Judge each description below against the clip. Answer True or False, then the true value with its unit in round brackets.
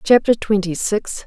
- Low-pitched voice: False (210 Hz)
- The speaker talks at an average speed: True (145 wpm)